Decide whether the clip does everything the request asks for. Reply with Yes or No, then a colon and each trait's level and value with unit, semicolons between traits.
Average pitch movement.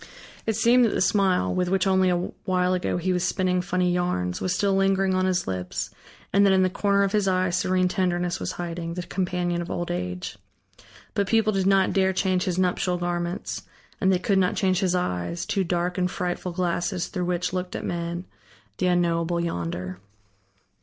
No: narrow, 1.4 semitones